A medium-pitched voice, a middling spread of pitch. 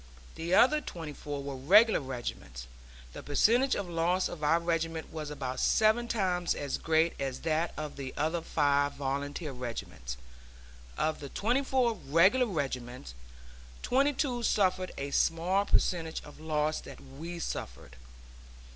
Yes: medium, 160 Hz; average, 5.0 semitones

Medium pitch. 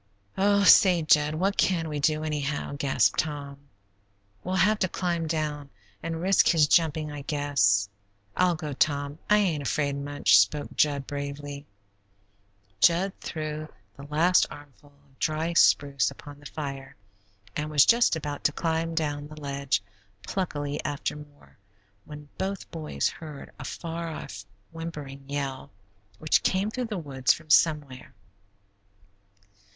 Yes: medium, 150 Hz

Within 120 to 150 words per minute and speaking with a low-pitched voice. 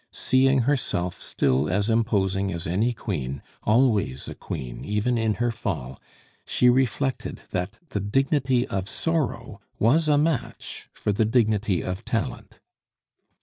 Yes: slow, 135 wpm; low, 110 Hz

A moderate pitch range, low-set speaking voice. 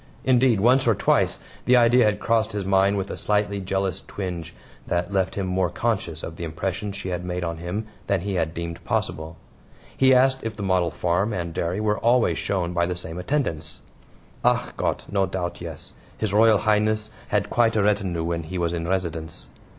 Yes: average, 3.7 semitones; very low, 95 Hz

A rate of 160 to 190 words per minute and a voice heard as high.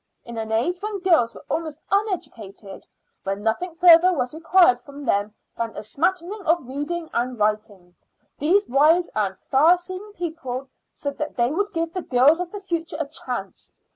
Yes: average, 170 wpm; very high, 300 Hz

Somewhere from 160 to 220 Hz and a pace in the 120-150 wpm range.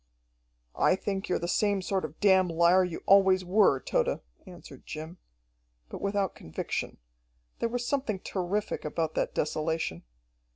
Yes: medium, 185 Hz; average, 140 wpm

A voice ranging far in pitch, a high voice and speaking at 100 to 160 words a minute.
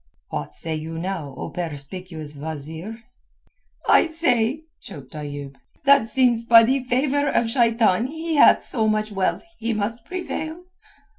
Yes: wide, 8.2 semitones; high, 220 Hz; average, 140 wpm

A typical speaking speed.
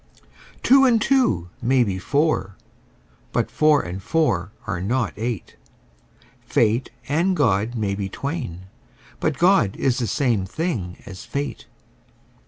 No: slow, 130 wpm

